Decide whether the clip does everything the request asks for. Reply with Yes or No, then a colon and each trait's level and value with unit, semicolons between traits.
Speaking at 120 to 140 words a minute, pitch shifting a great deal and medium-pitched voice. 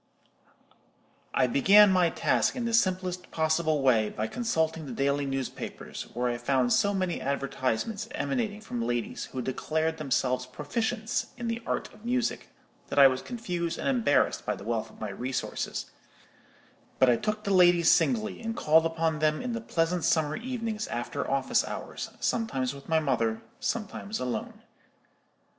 No: average, 160 wpm; wide, 8.5 semitones; medium, 160 Hz